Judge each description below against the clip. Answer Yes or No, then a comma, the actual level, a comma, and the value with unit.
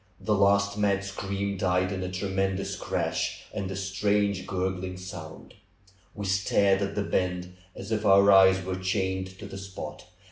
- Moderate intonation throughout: No, narrow, 1.2 semitones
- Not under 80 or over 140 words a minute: No, average, 165 wpm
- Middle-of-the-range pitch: No, very low, 95 Hz